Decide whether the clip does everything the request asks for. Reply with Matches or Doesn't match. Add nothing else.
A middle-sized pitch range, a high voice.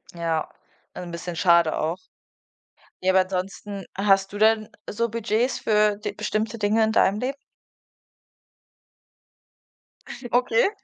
Matches